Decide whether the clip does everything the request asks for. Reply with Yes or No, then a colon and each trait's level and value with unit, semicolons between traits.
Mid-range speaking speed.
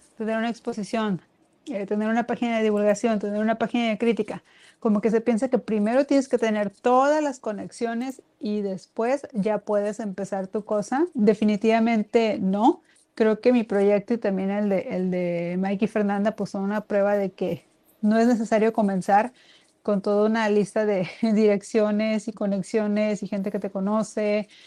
Yes: average, 170 wpm